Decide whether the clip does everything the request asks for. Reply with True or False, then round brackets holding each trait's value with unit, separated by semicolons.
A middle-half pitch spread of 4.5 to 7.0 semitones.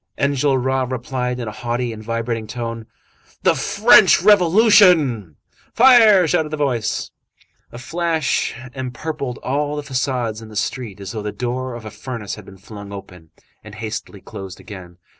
True (5.1 semitones)